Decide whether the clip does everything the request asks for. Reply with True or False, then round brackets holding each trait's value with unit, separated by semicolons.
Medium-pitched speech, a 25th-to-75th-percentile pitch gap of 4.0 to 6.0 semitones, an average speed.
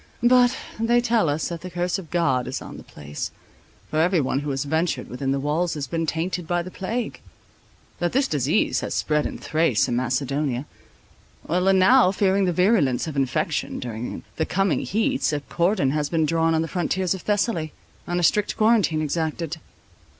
True (165 Hz; 4.6 semitones; 185 wpm)